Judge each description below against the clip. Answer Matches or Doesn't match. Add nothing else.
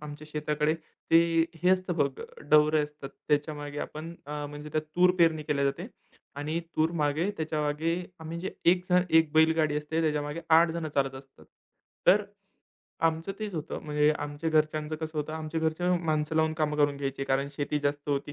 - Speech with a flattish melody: Matches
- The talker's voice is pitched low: Doesn't match